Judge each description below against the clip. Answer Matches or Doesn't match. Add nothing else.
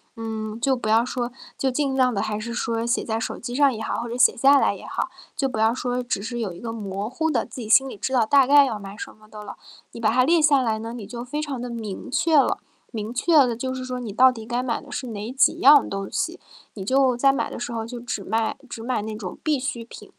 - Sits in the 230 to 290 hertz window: Matches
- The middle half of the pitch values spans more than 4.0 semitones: Doesn't match